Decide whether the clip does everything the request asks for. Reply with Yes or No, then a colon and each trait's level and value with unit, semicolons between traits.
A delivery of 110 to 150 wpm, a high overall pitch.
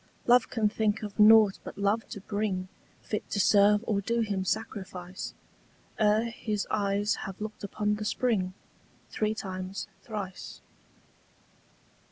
Yes: slow, 135 wpm; high, 210 Hz